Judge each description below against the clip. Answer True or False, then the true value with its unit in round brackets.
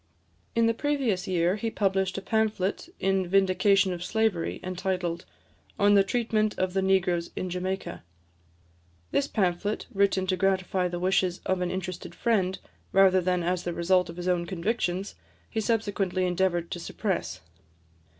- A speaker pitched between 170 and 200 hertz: True (190 Hz)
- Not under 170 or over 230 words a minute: False (150 wpm)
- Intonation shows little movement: True (2.0 semitones)